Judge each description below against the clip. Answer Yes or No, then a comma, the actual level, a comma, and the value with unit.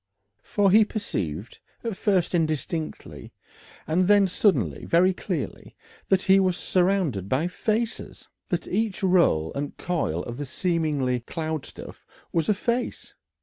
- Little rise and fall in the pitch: No, average, 5.3 semitones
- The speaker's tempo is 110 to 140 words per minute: Yes, slow, 135 wpm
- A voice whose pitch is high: No, medium, 175 Hz